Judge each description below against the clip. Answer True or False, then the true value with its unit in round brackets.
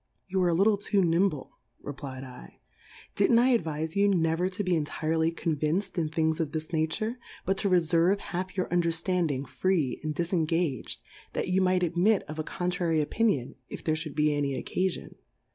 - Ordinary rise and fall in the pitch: True (3.1 semitones)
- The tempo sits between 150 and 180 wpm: False (190 wpm)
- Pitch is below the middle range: False (170 Hz)